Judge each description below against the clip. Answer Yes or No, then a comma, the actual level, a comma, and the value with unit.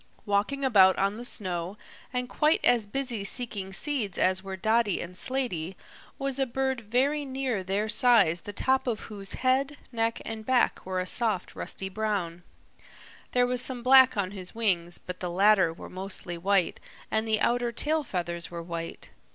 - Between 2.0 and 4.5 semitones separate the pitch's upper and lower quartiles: No, average, 5.0 semitones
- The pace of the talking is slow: No, average, 175 wpm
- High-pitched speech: Yes, high, 215 Hz